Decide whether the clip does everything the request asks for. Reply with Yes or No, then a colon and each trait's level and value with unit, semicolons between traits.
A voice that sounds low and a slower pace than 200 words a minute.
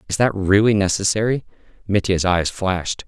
Yes: low, 100 Hz; slow, 135 wpm